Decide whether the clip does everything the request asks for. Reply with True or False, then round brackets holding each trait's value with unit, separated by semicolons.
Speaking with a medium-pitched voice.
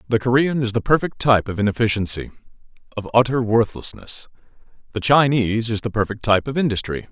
False (115 Hz)